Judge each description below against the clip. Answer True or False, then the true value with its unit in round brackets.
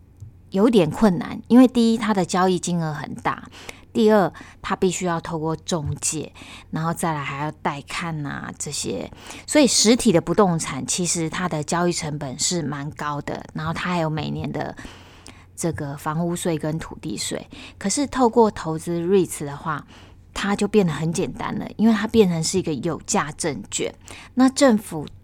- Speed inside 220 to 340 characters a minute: True (265 characters per minute)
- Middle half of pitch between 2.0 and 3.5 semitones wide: False (5.5 semitones)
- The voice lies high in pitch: False (170 Hz)